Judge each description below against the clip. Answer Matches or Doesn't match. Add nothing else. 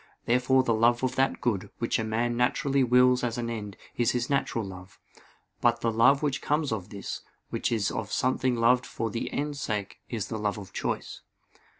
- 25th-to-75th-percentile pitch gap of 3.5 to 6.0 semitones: Doesn't match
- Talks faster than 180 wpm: Matches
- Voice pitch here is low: Matches